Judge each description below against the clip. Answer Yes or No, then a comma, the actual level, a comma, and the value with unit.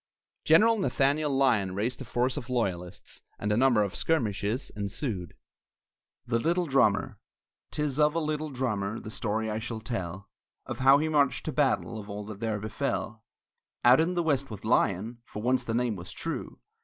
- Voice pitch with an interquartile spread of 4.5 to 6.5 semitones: Yes, average, 5.2 semitones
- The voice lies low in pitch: Yes, low, 120 Hz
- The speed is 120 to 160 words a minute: No, average, 180 wpm